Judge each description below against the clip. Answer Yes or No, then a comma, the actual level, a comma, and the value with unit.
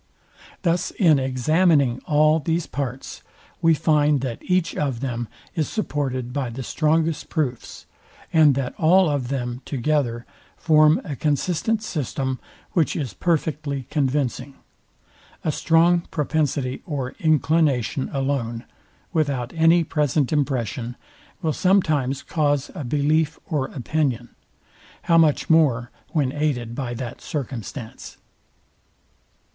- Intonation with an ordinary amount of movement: Yes, average, 3.5 semitones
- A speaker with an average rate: No, slow, 115 wpm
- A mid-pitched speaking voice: Yes, medium, 145 Hz